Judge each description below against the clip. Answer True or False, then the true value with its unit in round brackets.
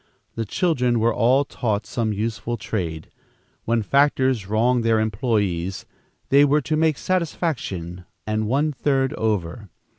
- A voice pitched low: True (115 Hz)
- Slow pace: True (130 wpm)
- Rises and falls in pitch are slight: False (4.6 semitones)